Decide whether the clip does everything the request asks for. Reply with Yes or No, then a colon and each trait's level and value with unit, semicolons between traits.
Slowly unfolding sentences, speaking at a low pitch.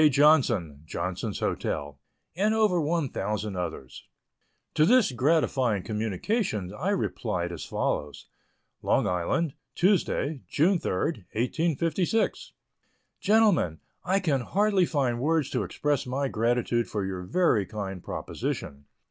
Yes: slow, 115 wpm; low, 130 Hz